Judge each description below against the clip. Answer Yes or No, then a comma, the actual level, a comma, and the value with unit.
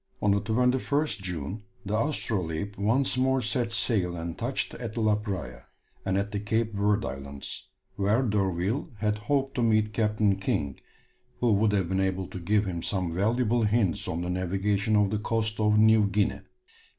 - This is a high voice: No, low, 105 Hz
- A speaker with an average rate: Yes, average, 175 wpm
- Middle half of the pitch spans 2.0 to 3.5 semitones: Yes, average, 2.8 semitones